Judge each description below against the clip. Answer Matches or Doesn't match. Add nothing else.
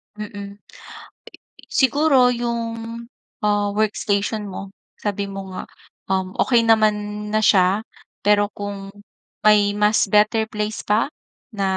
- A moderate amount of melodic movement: Doesn't match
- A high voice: Matches